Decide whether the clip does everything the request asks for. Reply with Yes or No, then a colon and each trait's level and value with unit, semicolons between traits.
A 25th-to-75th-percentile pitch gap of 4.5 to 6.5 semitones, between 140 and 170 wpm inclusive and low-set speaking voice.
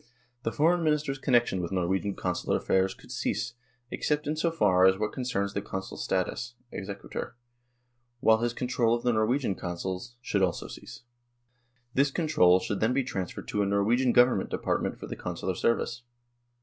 Yes: average, 5.0 semitones; average, 165 wpm; low, 115 Hz